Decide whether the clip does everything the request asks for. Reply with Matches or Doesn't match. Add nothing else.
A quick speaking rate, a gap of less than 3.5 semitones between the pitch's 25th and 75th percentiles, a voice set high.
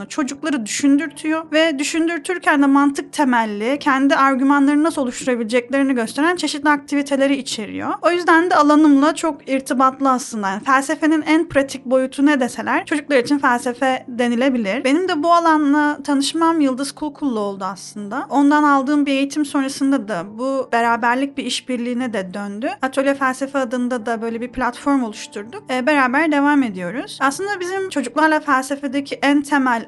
Matches